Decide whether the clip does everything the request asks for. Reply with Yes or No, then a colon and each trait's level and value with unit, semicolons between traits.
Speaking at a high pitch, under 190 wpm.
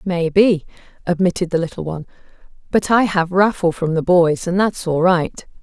No: medium, 175 Hz; average, 170 wpm